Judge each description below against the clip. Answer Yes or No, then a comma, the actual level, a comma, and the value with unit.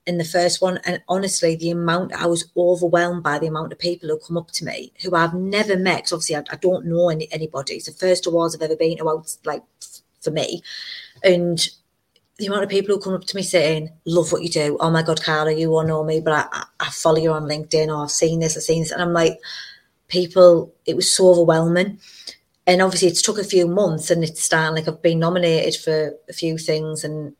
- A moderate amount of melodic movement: No, narrow, 2.2 semitones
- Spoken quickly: Yes, fast, 235 wpm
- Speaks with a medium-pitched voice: Yes, medium, 170 Hz